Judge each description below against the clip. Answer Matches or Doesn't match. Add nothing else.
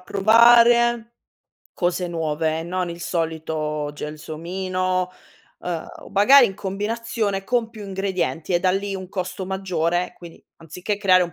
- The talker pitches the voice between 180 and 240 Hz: Matches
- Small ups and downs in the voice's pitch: Doesn't match